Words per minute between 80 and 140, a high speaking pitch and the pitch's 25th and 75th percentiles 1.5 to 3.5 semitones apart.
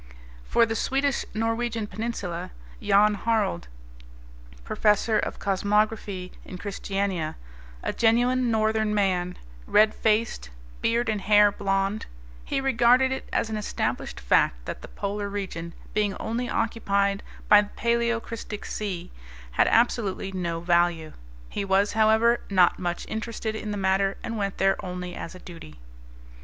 Yes: slow, 135 wpm; high, 210 Hz; average, 2.9 semitones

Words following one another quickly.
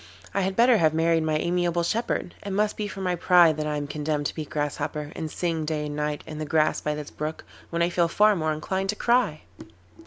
Yes: fast, 245 wpm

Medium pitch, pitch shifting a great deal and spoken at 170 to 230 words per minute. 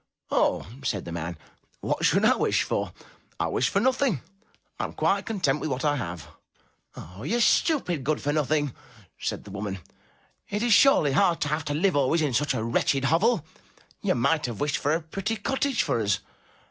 Yes: medium, 150 Hz; wide, 8.1 semitones; average, 195 wpm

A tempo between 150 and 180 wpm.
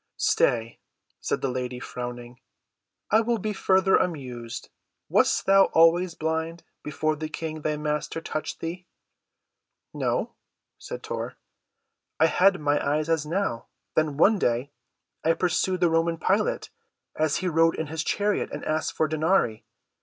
No: average, 140 wpm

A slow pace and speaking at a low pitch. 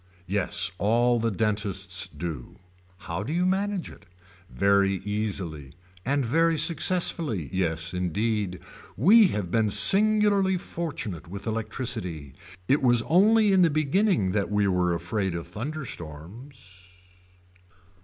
Yes: slow, 120 wpm; low, 105 Hz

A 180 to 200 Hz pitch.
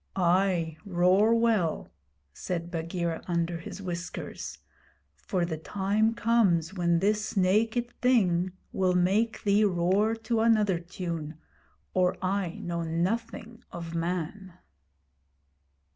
Yes: medium, 185 Hz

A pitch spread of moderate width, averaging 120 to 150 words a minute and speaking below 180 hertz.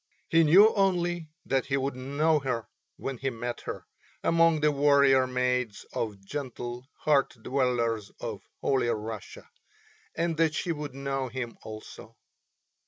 Yes: average, 3.8 semitones; average, 140 wpm; low, 135 Hz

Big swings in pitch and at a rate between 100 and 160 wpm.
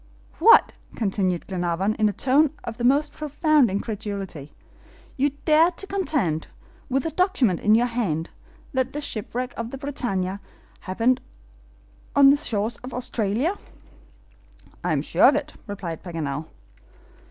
Yes: wide, 6.4 semitones; average, 140 wpm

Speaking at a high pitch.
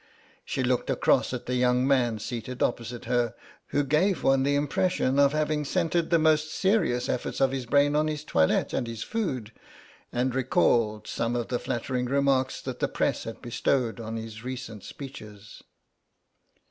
No: low, 130 Hz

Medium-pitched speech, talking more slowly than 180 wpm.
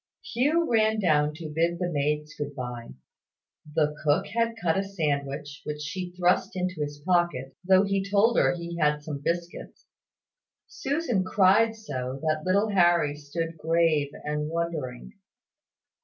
Yes: medium, 170 Hz; average, 145 wpm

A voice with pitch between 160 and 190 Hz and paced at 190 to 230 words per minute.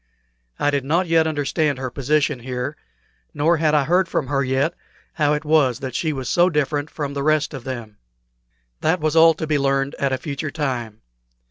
No: medium, 145 Hz; average, 200 wpm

